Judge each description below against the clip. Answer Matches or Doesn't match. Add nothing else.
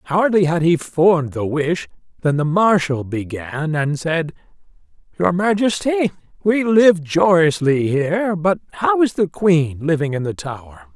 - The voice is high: Doesn't match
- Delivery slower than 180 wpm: Matches